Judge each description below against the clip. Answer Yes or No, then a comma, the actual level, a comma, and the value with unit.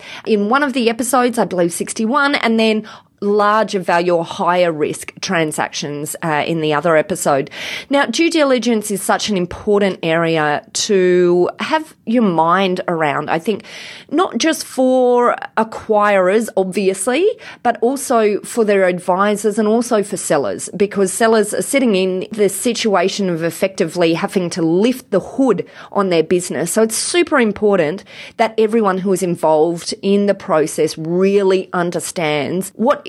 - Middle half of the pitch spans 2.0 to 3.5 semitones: No, average, 4.3 semitones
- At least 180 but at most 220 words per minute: No, average, 150 wpm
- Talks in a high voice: Yes, high, 200 Hz